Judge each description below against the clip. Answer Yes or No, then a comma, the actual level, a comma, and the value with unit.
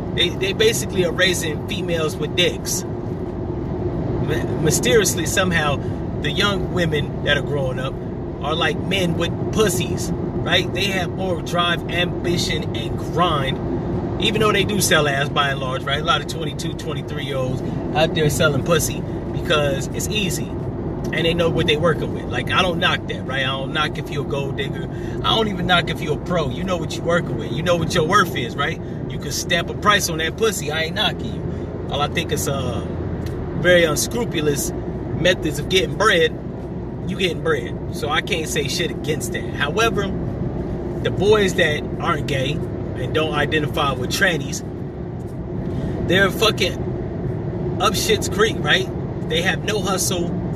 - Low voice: No, medium, 155 Hz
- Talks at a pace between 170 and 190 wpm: Yes, average, 180 wpm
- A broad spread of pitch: No, average, 4.2 semitones